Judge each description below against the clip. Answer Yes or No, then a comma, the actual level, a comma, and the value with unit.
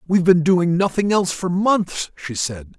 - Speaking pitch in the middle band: Yes, medium, 175 Hz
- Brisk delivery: No, average, 195 wpm